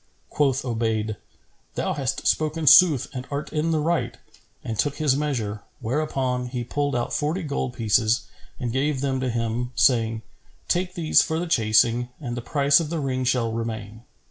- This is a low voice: Yes, low, 130 Hz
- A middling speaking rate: Yes, average, 170 wpm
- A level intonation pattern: No, average, 4.3 semitones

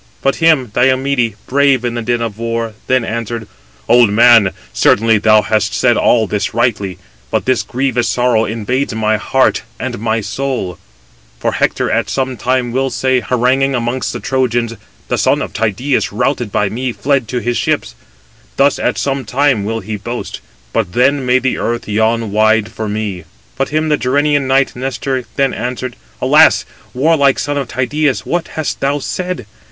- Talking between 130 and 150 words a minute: No, average, 170 wpm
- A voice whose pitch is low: Yes, low, 125 Hz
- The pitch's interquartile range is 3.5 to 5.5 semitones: No, average, 3.1 semitones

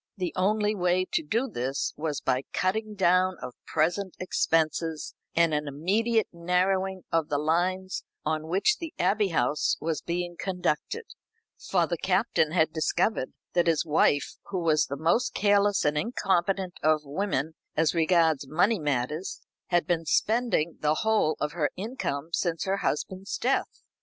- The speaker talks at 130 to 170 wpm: Yes, average, 155 wpm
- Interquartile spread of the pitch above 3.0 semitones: Yes, average, 3.9 semitones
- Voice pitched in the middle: Yes, medium, 175 Hz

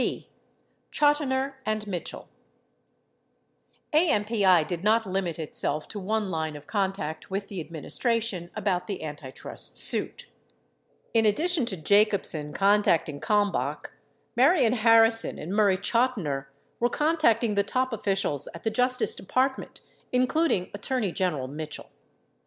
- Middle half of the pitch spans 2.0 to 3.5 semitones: No, wide, 5.4 semitones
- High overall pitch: Yes, high, 205 Hz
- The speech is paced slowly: Yes, slow, 130 wpm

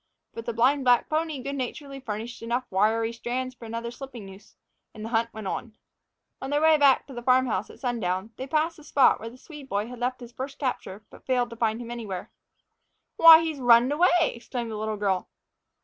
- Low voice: No, high, 240 Hz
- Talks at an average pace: No, fast, 210 wpm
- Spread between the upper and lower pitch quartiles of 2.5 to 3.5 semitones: Yes, average, 3.2 semitones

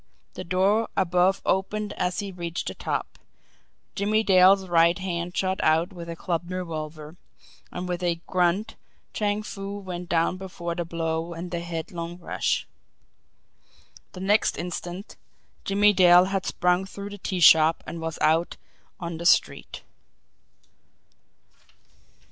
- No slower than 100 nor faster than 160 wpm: Yes, slow, 135 wpm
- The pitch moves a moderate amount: No, narrow, 2.2 semitones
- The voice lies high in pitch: No, medium, 180 Hz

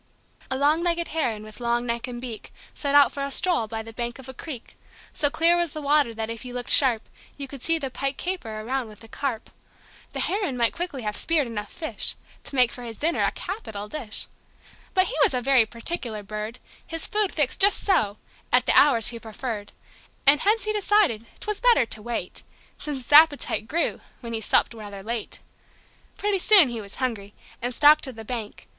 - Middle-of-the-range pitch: No, very high, 255 Hz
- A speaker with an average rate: No, fast, 210 wpm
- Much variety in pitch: Yes, wide, 5.8 semitones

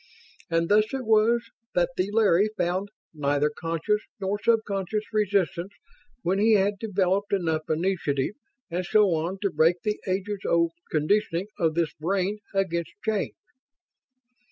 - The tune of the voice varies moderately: Yes, average, 3.7 semitones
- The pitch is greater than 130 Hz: Yes, high, 190 Hz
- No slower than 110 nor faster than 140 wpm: Yes, slow, 135 wpm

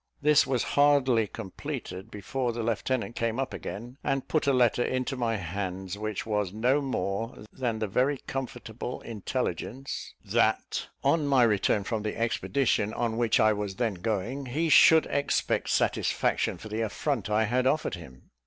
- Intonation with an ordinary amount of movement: Yes, average, 4.1 semitones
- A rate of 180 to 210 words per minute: No, average, 160 wpm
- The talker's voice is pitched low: Yes, low, 115 Hz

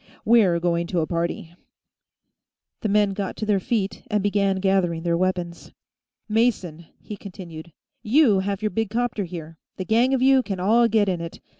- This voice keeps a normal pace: Yes, average, 175 wpm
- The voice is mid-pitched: No, high, 195 Hz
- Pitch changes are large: No, average, 4.1 semitones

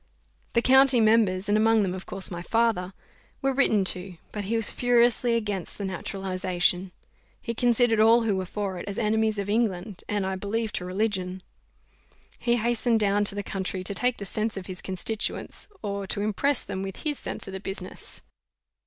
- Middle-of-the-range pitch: No, high, 205 Hz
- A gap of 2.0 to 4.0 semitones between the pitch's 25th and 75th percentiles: Yes, average, 3.1 semitones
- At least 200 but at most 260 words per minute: No, average, 190 wpm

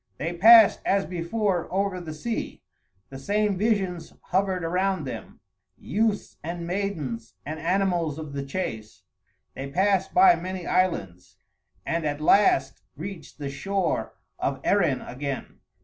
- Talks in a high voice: No, medium, 180 Hz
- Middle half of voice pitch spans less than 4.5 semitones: No, average, 4.8 semitones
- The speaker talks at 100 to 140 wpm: Yes, slow, 135 wpm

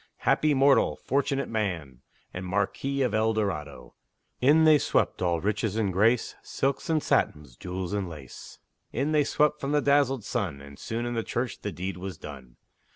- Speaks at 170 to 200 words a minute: Yes, average, 175 wpm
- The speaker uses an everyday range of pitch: No, wide, 7.4 semitones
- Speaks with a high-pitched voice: No, low, 110 Hz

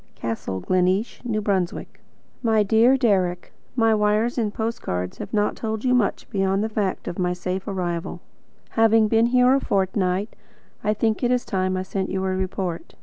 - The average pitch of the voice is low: No, high, 205 Hz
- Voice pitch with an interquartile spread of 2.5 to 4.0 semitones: Yes, average, 3.2 semitones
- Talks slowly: No, average, 180 wpm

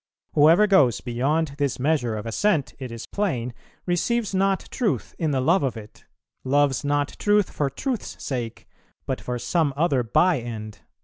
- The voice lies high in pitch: No, medium, 145 Hz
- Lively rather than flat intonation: Yes, wide, 6.3 semitones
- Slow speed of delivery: No, average, 165 wpm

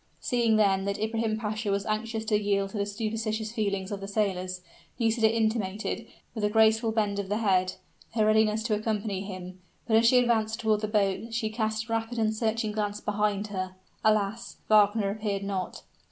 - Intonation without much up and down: Yes, narrow, 1.7 semitones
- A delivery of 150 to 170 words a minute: No, average, 185 wpm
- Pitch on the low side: No, high, 215 Hz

